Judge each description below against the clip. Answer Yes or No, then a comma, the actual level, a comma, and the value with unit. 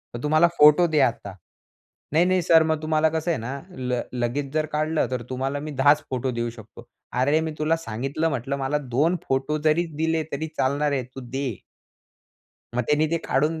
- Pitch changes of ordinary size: Yes, average, 3.2 semitones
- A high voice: No, medium, 150 Hz